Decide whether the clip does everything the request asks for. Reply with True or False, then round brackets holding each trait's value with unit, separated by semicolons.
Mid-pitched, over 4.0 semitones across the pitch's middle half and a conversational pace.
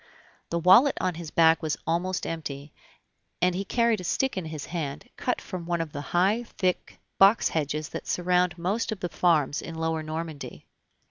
False (170 Hz; 2.8 semitones; 185 wpm)